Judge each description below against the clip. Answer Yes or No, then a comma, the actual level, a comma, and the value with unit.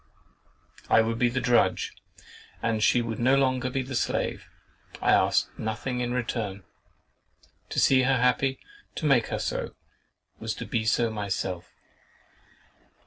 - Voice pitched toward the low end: Yes, low, 120 Hz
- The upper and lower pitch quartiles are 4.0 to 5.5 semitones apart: No, narrow, 2.5 semitones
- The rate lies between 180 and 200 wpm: No, average, 140 wpm